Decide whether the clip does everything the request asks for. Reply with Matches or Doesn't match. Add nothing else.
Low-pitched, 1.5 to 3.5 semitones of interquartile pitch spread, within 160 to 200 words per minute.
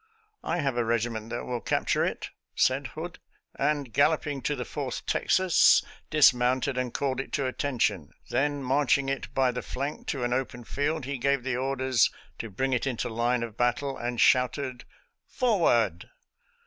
Matches